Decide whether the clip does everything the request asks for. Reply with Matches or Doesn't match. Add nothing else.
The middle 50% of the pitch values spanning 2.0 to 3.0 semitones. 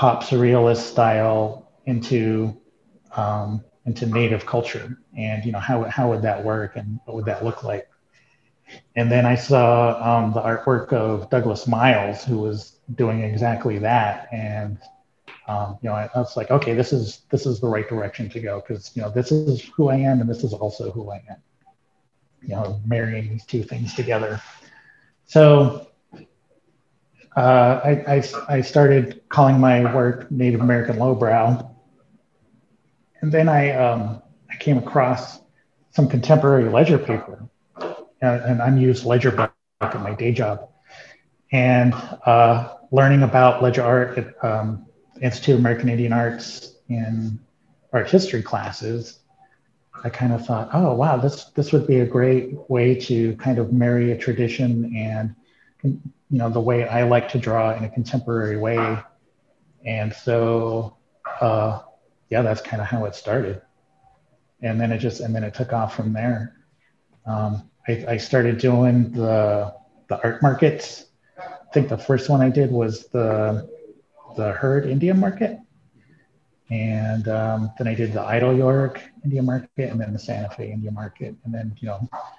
Matches